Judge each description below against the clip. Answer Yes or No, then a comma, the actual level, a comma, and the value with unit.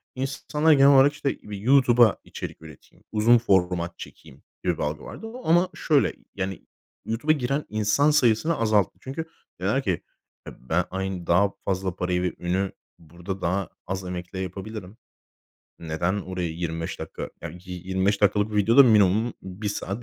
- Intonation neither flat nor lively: Yes, average, 5.0 semitones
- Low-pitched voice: Yes, low, 100 Hz